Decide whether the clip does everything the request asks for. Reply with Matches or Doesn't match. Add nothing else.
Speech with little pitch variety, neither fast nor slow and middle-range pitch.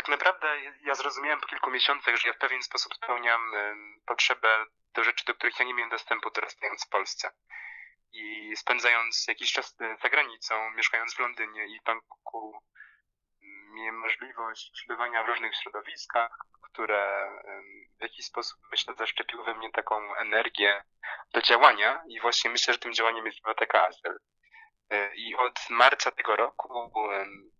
Doesn't match